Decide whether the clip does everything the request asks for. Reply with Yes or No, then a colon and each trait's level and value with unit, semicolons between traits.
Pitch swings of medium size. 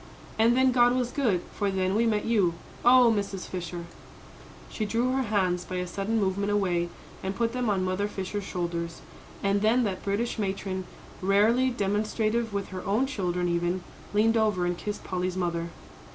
Yes: average, 3.6 semitones